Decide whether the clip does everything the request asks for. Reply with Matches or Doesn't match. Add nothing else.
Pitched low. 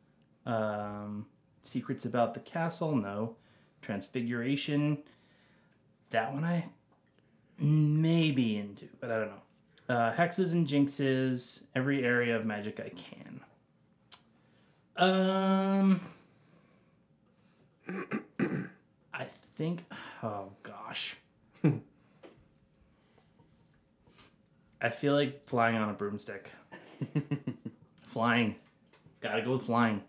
Matches